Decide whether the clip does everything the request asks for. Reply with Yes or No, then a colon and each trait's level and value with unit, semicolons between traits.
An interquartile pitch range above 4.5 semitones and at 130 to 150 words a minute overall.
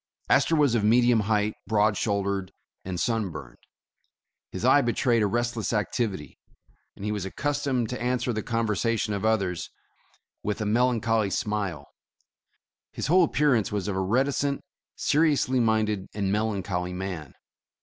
No: average, 3.4 semitones; average, 140 wpm